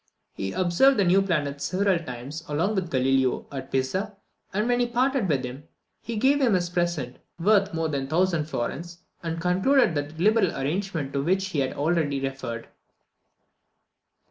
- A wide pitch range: Yes, wide, 5.8 semitones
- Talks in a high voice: No, medium, 170 Hz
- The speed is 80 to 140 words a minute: No, average, 165 wpm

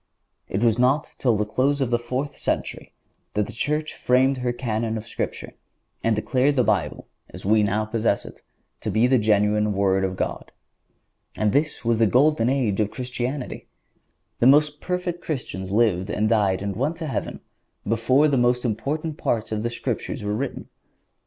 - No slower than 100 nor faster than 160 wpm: No, average, 180 wpm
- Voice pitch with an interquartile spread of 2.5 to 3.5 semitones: No, average, 4.2 semitones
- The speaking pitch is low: Yes, low, 120 Hz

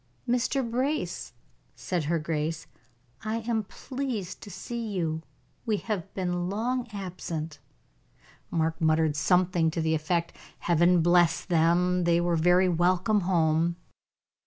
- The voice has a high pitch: No, medium, 175 Hz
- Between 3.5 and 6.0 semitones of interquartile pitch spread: Yes, average, 3.8 semitones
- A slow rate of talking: Yes, slow, 125 wpm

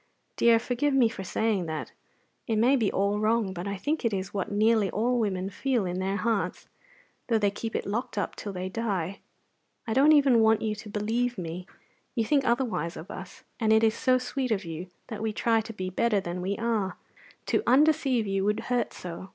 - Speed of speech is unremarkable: No, fast, 210 wpm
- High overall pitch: Yes, high, 220 Hz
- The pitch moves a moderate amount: Yes, average, 3.5 semitones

